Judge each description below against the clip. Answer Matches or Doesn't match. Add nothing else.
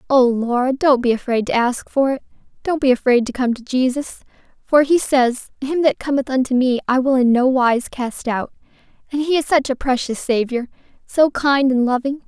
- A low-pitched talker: Doesn't match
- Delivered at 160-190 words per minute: Doesn't match